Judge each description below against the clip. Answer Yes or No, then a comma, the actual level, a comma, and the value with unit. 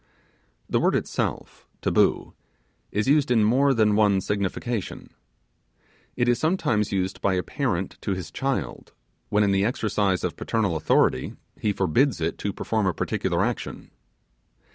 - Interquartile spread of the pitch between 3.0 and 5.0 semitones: Yes, average, 4.1 semitones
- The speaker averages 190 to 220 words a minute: No, average, 145 wpm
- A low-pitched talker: Yes, low, 105 Hz